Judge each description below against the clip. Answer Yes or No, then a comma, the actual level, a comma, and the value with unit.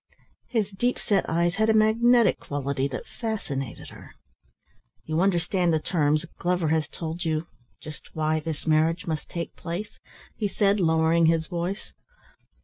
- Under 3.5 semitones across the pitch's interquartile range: No, average, 3.9 semitones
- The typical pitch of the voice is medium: Yes, medium, 170 Hz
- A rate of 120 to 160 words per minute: Yes, average, 145 wpm